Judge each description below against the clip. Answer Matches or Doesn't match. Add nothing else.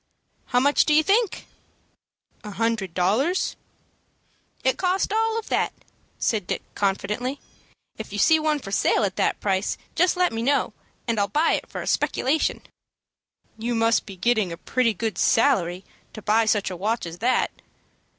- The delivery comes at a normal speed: Matches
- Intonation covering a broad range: Matches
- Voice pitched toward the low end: Doesn't match